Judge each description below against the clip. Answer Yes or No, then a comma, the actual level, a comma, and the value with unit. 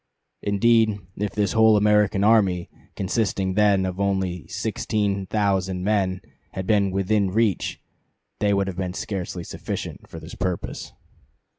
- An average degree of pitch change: No, narrow, 2.0 semitones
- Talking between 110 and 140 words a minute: Yes, slow, 135 wpm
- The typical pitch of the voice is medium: No, low, 100 Hz